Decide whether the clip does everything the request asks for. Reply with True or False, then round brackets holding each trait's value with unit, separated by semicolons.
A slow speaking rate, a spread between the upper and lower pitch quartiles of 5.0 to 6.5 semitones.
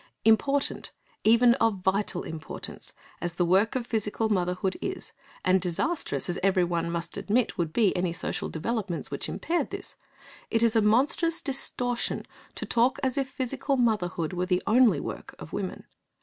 False (160 wpm; 5.5 semitones)